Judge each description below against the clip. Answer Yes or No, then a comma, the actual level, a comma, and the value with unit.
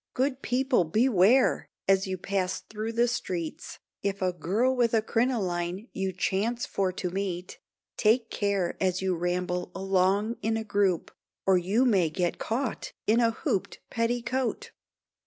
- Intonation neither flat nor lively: Yes, average, 4.1 semitones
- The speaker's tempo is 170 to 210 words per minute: No, average, 150 wpm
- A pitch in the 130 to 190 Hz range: No, high, 200 Hz